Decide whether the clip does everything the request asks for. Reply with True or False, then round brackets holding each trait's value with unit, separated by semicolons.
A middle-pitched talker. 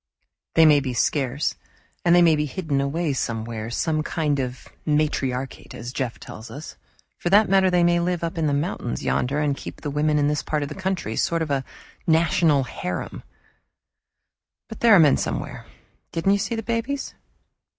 True (150 Hz)